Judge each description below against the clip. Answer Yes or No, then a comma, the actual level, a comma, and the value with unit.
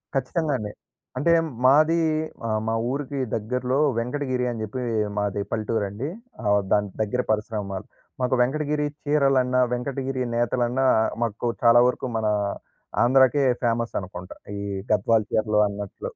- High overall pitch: No, low, 120 Hz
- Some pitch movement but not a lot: Yes, average, 3.7 semitones